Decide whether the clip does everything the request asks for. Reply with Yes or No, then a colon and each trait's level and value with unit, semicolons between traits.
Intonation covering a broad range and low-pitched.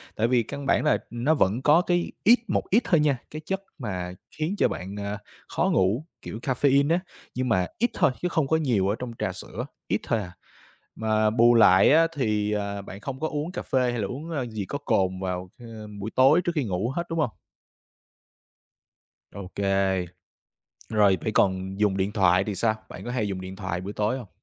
Yes: wide, 6.5 semitones; low, 110 Hz